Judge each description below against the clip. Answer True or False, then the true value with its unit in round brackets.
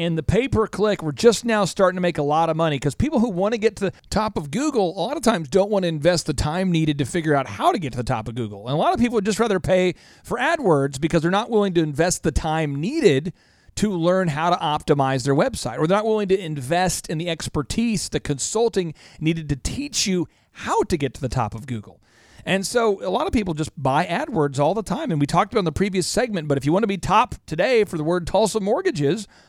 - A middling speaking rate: False (270 wpm)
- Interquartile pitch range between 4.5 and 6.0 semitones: True (5.5 semitones)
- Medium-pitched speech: True (170 Hz)